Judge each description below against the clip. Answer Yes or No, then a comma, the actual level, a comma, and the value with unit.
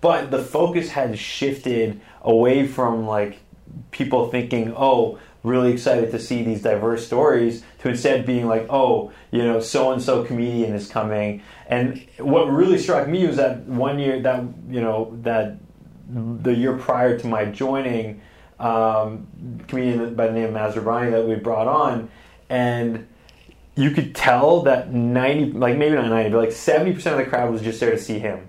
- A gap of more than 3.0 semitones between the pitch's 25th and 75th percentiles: No, narrow, 2.6 semitones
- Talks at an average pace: Yes, average, 175 wpm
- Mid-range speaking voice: No, low, 120 Hz